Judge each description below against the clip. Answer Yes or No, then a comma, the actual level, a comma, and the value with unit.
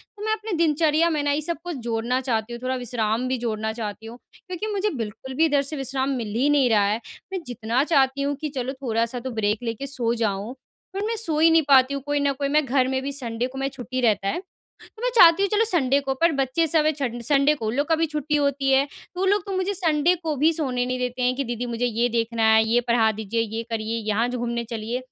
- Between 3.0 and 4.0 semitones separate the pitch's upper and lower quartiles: No, average, 4.5 semitones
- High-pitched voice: Yes, very high, 260 Hz